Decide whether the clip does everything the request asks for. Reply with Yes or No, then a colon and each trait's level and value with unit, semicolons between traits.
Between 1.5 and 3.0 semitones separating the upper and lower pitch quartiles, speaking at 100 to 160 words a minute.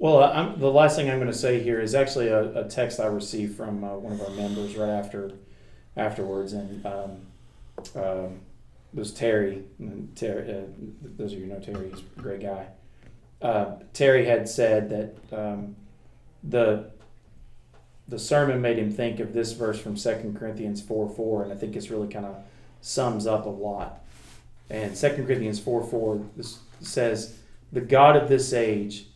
No: narrow, 2.6 semitones; average, 180 wpm